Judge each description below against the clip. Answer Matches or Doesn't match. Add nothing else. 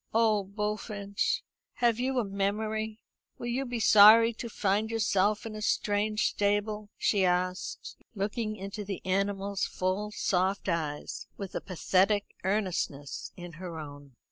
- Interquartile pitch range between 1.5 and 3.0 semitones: Matches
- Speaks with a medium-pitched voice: Doesn't match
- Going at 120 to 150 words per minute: Matches